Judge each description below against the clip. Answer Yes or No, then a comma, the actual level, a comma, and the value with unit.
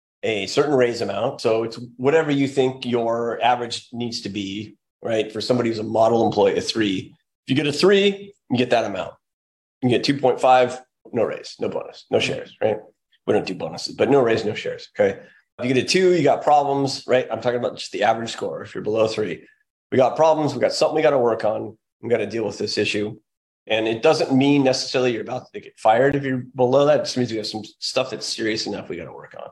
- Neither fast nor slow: No, fast, 245 wpm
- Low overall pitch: Yes, low, 125 Hz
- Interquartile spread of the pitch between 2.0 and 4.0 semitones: No, average, 4.4 semitones